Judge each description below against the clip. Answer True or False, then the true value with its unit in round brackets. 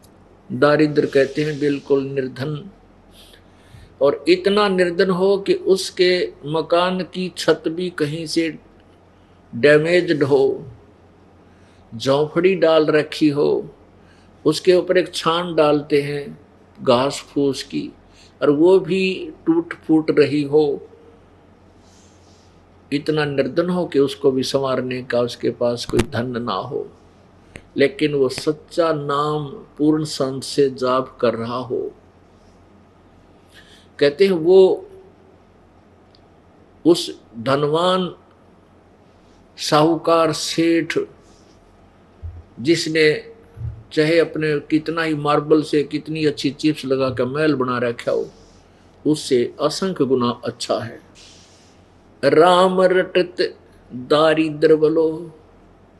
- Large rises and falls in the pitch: True (8.0 semitones)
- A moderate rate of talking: False (105 wpm)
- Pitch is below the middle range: False (145 Hz)